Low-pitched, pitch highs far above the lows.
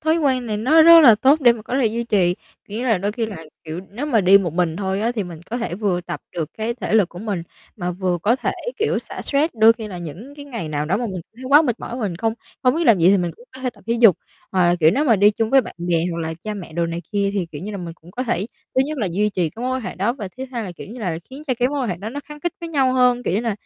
No: high, 215 Hz; wide, 5.9 semitones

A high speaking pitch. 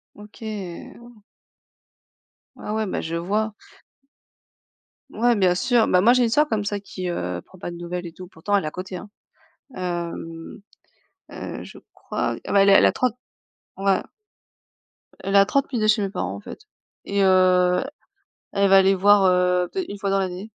Yes: high, 195 Hz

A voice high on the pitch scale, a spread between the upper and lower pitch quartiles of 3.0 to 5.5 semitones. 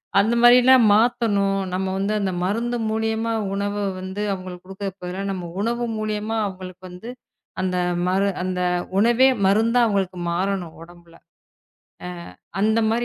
Yes: high, 200 Hz; average, 3.3 semitones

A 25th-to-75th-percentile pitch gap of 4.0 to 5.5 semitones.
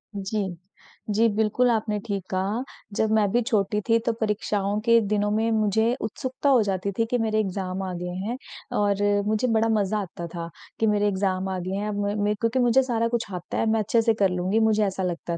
No: narrow, 2.6 semitones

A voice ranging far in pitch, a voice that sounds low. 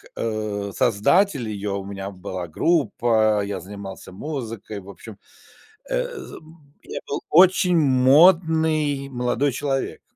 Yes: wide, 7.3 semitones; low, 125 Hz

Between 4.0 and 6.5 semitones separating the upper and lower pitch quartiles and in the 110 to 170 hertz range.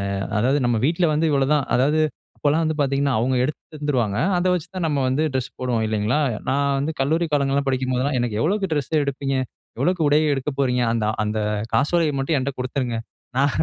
No: average, 2.8 semitones; medium, 140 Hz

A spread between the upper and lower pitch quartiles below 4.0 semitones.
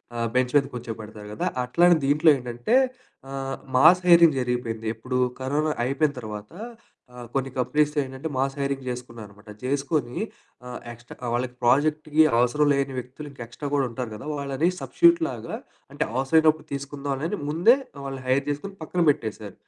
Yes: average, 3.5 semitones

